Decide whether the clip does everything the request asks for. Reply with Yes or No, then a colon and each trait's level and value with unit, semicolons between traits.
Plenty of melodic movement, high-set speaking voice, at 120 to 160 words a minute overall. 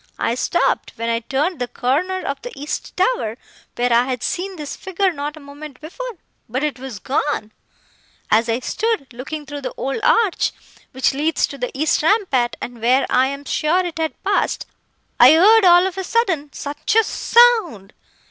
No: wide, 6.5 semitones; very high, 295 Hz; average, 180 wpm